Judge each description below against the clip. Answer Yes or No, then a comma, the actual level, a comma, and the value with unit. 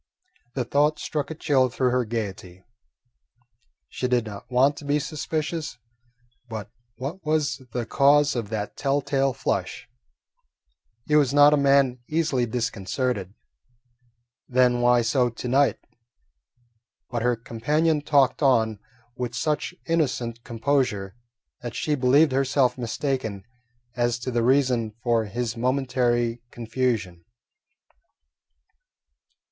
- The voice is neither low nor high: No, low, 125 Hz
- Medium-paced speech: No, slow, 120 wpm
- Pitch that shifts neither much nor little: Yes, average, 3.4 semitones